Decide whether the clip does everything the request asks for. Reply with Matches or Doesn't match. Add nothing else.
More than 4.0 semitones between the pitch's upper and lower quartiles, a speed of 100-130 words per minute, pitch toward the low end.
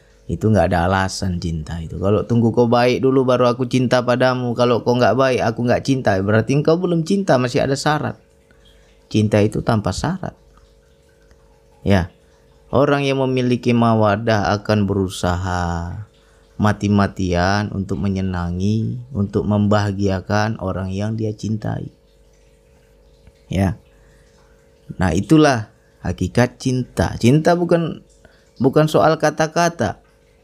Matches